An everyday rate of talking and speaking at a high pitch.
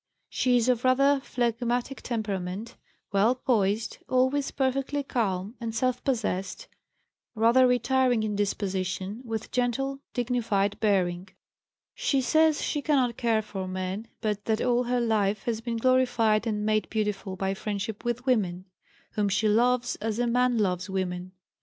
Yes: average, 145 wpm; high, 225 Hz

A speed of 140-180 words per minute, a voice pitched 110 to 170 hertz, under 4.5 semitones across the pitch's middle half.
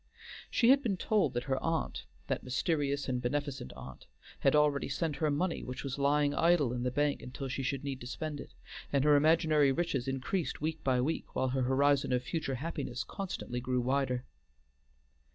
No: average, 190 wpm; medium, 140 Hz; average, 3.2 semitones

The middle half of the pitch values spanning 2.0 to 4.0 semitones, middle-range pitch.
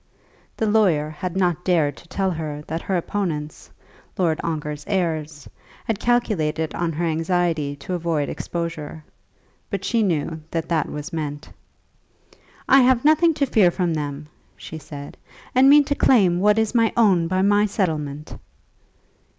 No: average, 4.9 semitones; medium, 170 Hz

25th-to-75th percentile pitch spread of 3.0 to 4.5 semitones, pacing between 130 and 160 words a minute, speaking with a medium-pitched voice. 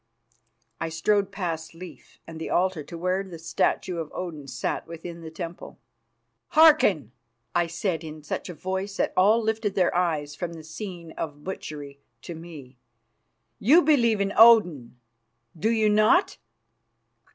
Yes: average, 4.0 semitones; average, 150 wpm; medium, 175 Hz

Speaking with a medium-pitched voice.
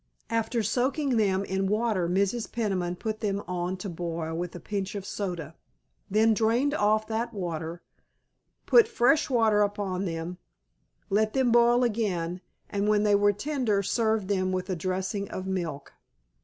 No: high, 205 Hz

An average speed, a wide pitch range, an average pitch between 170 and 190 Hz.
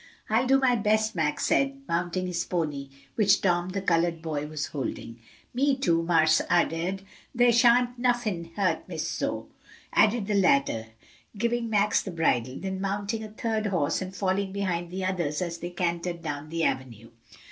No: average, 170 wpm; average, 4.5 semitones; medium, 185 Hz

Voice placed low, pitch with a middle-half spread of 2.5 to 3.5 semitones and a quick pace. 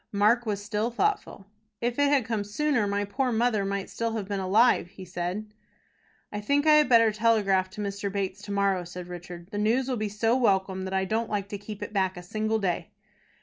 No: high, 205 Hz; average, 3.0 semitones; fast, 220 wpm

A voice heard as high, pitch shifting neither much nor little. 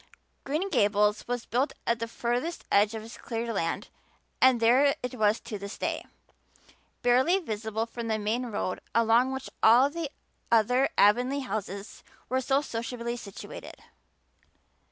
Yes: high, 235 Hz; average, 3.1 semitones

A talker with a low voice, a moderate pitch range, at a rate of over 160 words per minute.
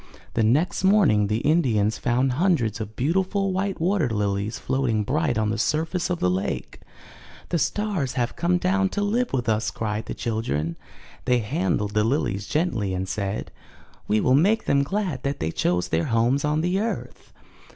No: low, 125 Hz; wide, 8.5 semitones; average, 180 wpm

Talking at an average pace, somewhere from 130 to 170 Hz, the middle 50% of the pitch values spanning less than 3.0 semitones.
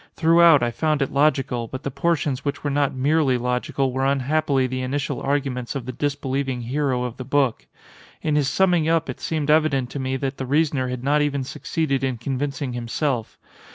Yes: average, 190 wpm; medium, 140 Hz; narrow, 2.5 semitones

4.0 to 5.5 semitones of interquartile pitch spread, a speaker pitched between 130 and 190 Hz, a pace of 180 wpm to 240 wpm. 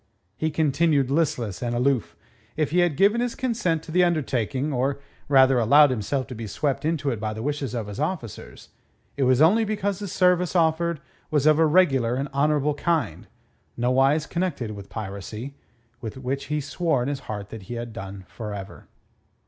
Yes: average, 5.2 semitones; medium, 140 Hz; average, 185 wpm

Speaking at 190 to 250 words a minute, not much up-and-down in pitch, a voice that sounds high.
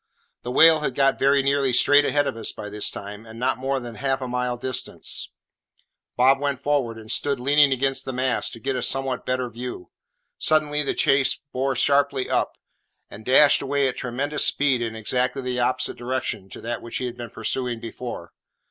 No: average, 195 wpm; narrow, 2.3 semitones; low, 130 Hz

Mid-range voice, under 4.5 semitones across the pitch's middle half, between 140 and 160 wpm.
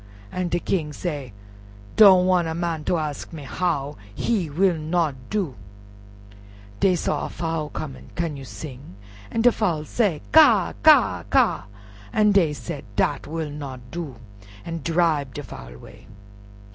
Yes: medium, 160 Hz; average, 3.7 semitones; average, 150 wpm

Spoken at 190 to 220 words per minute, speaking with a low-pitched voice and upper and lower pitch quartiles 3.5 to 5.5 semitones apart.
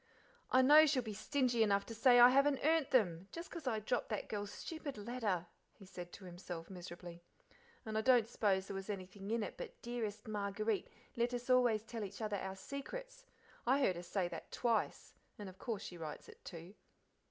No: average, 200 wpm; high, 215 Hz; average, 4.6 semitones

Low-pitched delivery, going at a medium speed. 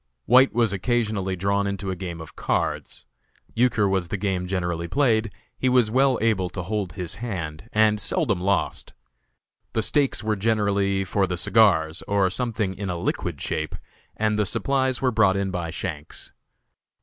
Yes: low, 100 Hz; average, 165 wpm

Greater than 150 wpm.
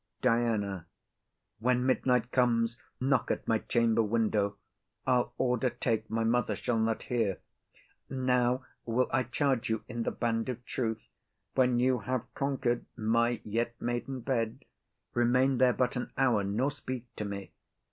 No: average, 145 wpm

